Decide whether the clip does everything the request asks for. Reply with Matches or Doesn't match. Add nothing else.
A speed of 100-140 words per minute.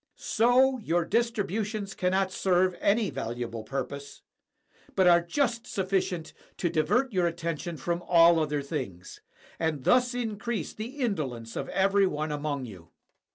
Matches